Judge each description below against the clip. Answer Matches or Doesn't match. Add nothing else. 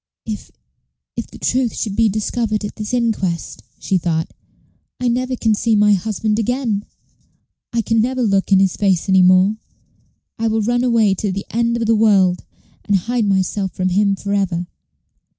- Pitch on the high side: Matches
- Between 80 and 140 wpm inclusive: Doesn't match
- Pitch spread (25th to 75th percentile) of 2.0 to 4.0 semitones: Matches